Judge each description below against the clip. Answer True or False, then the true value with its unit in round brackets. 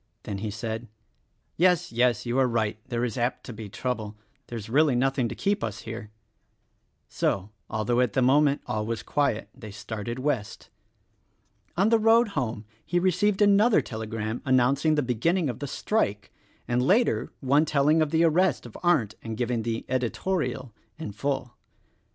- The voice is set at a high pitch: False (125 Hz)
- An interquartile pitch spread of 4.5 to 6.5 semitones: True (5.6 semitones)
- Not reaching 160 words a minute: False (170 wpm)